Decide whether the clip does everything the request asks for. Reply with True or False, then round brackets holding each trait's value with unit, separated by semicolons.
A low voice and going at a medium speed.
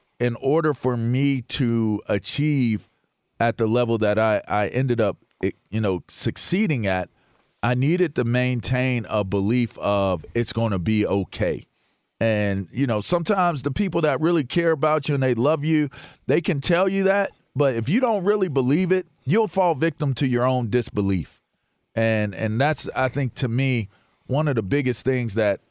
True (125 Hz; 180 wpm)